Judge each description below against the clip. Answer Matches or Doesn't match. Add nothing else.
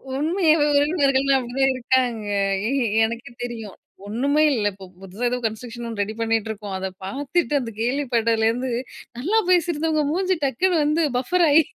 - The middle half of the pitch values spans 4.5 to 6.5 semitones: Matches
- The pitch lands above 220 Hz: Matches